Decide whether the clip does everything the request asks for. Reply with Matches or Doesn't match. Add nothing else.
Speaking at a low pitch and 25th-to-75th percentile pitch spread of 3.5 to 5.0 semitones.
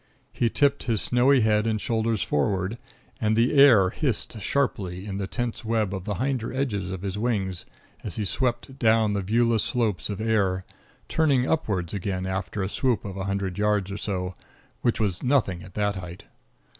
Matches